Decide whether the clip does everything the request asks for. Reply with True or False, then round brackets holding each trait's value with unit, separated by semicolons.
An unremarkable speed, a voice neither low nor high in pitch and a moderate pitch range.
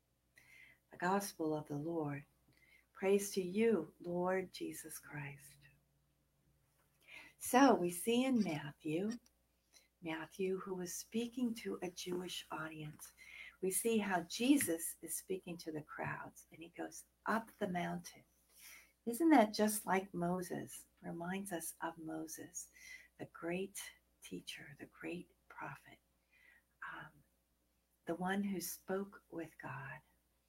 False (120 wpm; 175 Hz; 4.1 semitones)